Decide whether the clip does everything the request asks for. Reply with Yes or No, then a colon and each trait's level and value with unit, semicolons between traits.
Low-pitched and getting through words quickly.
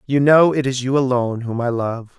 Yes: low, 130 Hz; fast, 245 wpm